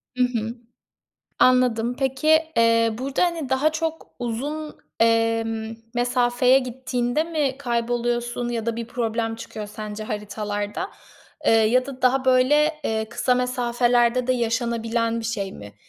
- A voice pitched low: No, high, 240 Hz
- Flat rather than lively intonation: Yes, narrow, 2.3 semitones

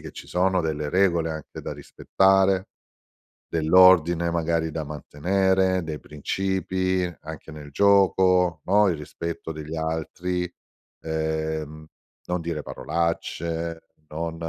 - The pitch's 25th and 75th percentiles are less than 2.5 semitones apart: No, average, 2.8 semitones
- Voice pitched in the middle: No, very low, 85 Hz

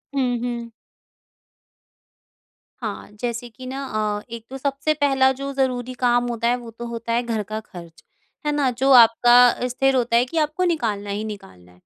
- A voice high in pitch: Yes, high, 245 Hz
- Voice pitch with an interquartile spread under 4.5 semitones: Yes, narrow, 2.6 semitones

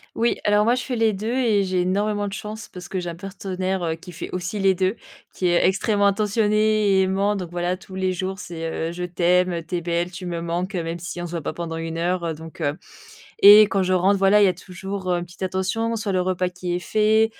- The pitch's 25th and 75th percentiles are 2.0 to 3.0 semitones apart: Yes, average, 2.7 semitones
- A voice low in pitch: No, medium, 185 Hz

